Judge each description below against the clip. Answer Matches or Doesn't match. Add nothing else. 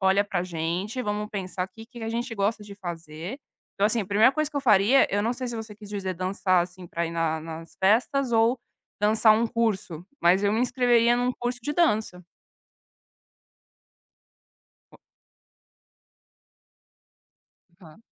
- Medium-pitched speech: Doesn't match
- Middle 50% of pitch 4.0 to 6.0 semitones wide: Matches